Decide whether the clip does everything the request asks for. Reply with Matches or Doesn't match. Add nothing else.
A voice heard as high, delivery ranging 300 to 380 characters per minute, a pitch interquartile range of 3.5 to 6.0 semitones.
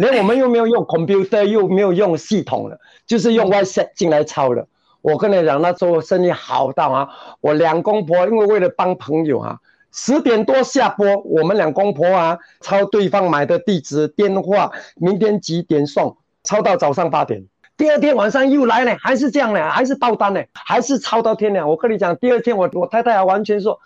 Matches